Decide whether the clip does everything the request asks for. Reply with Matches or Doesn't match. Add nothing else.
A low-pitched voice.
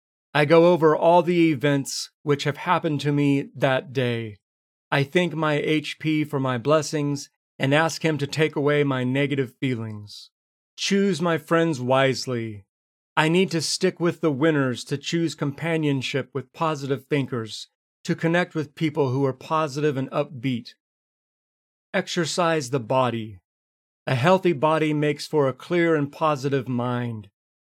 Doesn't match